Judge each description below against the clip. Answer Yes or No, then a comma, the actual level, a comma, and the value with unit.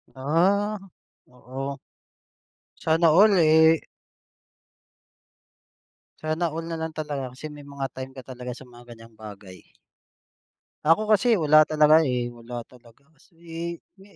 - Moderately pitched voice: Yes, medium, 150 Hz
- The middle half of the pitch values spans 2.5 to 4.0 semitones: No, average, 4.7 semitones